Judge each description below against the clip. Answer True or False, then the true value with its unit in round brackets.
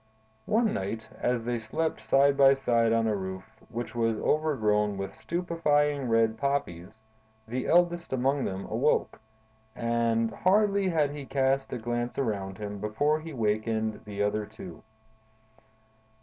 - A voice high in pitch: False (120 Hz)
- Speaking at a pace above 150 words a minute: False (140 wpm)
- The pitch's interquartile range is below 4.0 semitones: False (4.9 semitones)